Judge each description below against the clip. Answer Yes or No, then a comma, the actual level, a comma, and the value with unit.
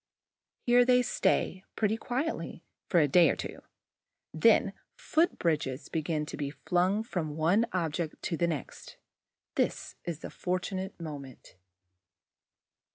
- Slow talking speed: Yes, slow, 130 wpm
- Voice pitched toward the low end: No, medium, 175 Hz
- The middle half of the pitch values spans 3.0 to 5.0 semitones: No, wide, 5.4 semitones